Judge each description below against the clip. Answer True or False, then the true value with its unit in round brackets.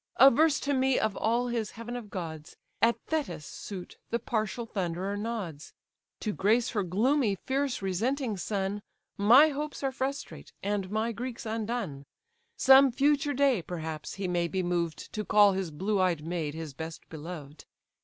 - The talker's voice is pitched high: True (210 Hz)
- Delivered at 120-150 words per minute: False (160 wpm)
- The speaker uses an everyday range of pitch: False (5.7 semitones)